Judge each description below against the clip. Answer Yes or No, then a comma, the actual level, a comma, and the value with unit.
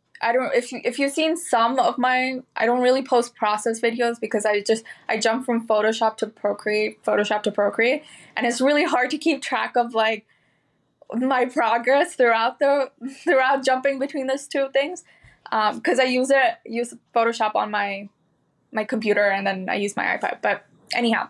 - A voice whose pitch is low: No, high, 240 Hz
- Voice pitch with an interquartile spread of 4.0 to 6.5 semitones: No, average, 3.5 semitones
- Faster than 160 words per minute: Yes, average, 185 wpm